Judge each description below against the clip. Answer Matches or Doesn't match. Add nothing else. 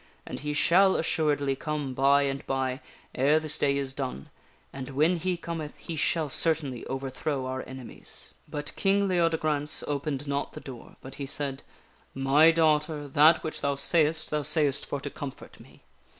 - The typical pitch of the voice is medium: Matches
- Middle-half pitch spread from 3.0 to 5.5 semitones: Doesn't match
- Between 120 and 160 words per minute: Doesn't match